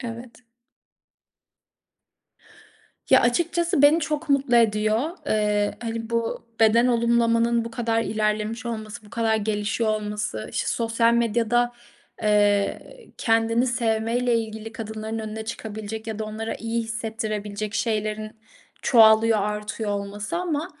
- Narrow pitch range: Yes, narrow, 1.6 semitones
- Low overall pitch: No, high, 225 Hz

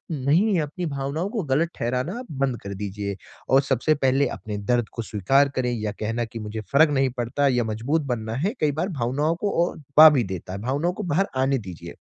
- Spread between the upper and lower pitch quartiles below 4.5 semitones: No, average, 5.3 semitones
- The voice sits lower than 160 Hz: Yes, low, 135 Hz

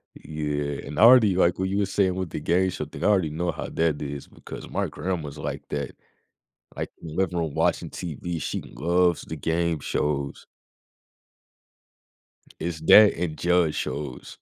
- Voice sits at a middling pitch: No, very low, 85 Hz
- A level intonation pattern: No, average, 3.5 semitones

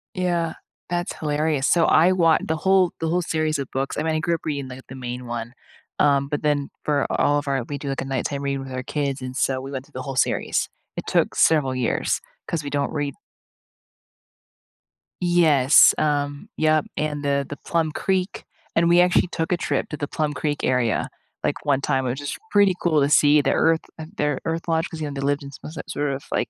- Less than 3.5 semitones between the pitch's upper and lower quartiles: Yes, average, 2.9 semitones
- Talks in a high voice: No, medium, 145 Hz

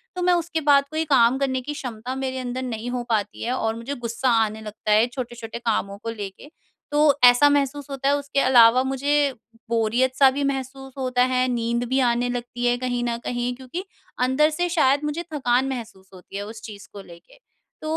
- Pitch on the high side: Yes, very high, 255 Hz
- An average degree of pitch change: Yes, average, 3.0 semitones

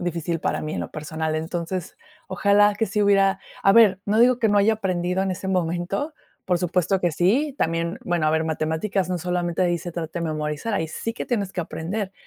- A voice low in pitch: No, medium, 180 Hz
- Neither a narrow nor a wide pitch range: Yes, average, 3.3 semitones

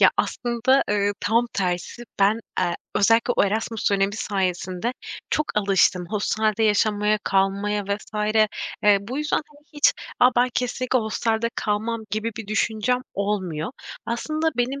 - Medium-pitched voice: No, high, 215 Hz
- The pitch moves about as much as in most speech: Yes, average, 3.0 semitones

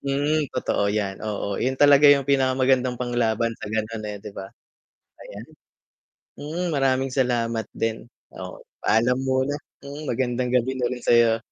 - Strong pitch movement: No, average, 2.9 semitones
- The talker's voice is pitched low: Yes, low, 125 Hz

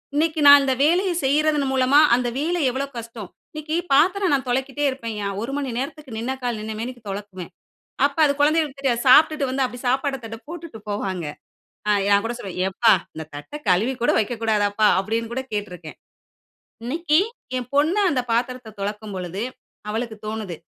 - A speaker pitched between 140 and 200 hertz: No, high, 245 Hz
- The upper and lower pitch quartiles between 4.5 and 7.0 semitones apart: Yes, average, 5.0 semitones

